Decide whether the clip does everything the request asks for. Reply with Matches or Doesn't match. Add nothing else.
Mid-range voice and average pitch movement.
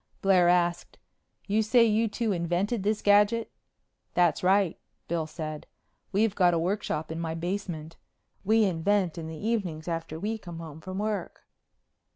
Matches